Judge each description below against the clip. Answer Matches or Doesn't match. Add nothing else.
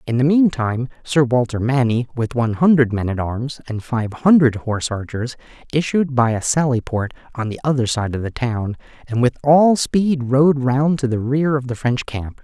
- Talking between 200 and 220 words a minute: Matches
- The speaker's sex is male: Matches